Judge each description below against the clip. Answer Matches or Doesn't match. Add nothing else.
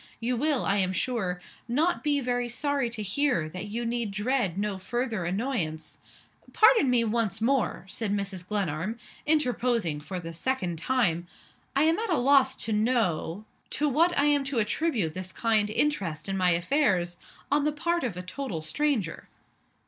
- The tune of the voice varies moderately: Doesn't match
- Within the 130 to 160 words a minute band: Doesn't match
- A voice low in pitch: Doesn't match